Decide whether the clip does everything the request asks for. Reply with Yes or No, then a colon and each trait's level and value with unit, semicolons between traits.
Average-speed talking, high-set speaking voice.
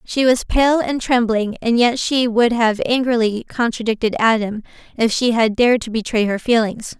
Yes: average, 180 wpm; high, 230 Hz